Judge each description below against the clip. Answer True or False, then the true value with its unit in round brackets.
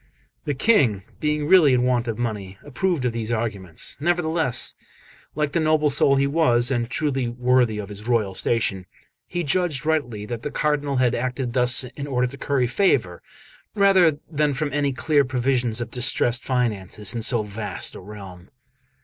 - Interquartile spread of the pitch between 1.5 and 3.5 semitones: False (4.1 semitones)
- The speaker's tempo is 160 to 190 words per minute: True (170 wpm)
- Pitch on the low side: True (125 Hz)